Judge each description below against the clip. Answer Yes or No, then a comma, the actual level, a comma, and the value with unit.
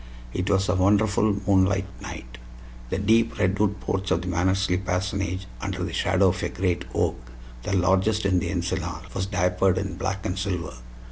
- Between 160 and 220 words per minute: Yes, average, 175 wpm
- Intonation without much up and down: Yes, narrow, 1.5 semitones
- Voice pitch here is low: Yes, very low, 95 Hz